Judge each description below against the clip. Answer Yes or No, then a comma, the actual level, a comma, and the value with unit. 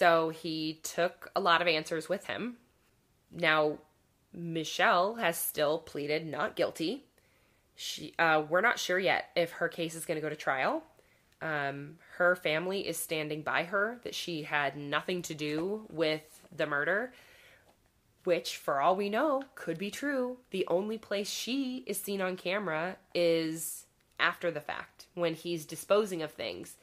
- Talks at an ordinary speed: Yes, average, 160 wpm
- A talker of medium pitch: Yes, medium, 170 Hz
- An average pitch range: Yes, average, 3.5 semitones